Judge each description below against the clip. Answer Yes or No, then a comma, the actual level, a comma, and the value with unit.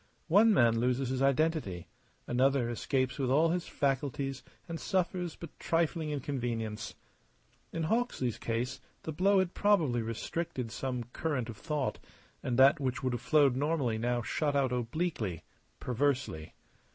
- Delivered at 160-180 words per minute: No, average, 140 wpm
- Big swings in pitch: No, average, 4.7 semitones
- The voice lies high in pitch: No, low, 135 Hz